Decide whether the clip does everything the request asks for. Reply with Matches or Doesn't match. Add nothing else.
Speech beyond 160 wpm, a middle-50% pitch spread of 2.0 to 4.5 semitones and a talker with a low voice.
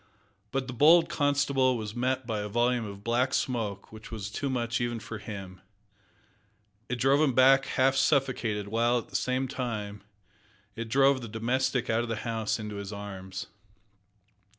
Matches